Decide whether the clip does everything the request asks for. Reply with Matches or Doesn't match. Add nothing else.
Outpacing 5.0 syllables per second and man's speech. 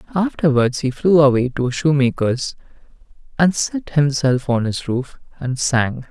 Doesn't match